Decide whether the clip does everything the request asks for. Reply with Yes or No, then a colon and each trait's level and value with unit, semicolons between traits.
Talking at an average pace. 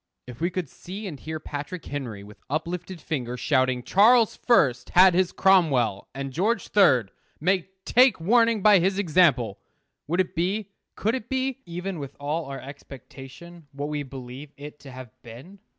Yes: average, 165 wpm